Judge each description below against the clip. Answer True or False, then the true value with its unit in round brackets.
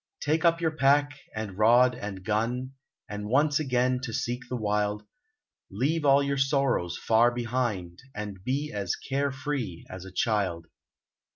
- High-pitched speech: False (120 Hz)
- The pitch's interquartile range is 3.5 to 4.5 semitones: False (4.9 semitones)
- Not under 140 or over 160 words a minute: True (150 wpm)